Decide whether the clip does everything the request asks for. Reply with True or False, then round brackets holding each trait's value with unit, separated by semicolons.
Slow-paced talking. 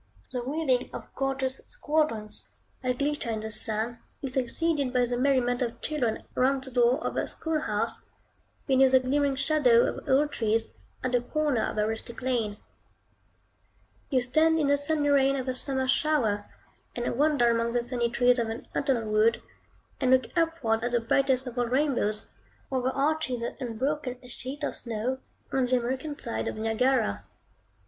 False (170 wpm)